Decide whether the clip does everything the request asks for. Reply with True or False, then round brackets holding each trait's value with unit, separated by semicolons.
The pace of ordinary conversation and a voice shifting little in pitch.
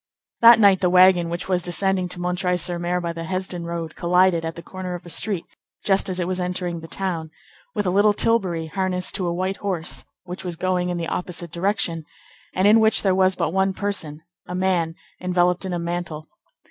False (210 wpm; 1.7 semitones)